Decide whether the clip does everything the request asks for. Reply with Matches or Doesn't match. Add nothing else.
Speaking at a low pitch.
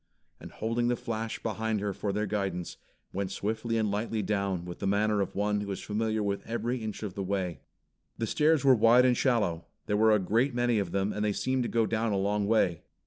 Matches